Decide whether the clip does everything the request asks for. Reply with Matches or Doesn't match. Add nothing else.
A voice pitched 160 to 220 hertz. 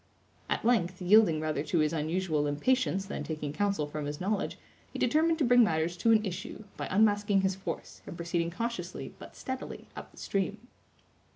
Matches